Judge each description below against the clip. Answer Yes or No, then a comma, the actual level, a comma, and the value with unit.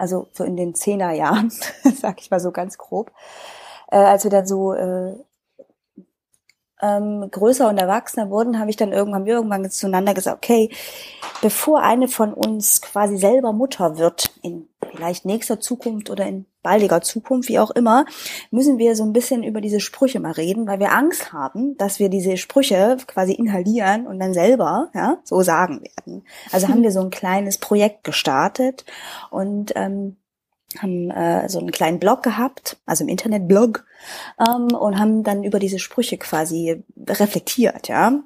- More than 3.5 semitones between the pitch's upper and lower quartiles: Yes, average, 3.9 semitones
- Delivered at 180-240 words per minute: No, average, 170 wpm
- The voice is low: No, high, 210 Hz